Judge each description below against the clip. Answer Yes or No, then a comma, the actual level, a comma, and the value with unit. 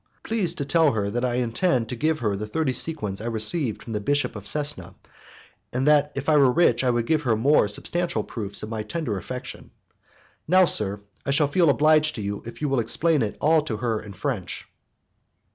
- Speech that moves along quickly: Yes, fast, 210 wpm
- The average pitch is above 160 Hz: No, low, 125 Hz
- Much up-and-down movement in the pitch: Yes, wide, 6.0 semitones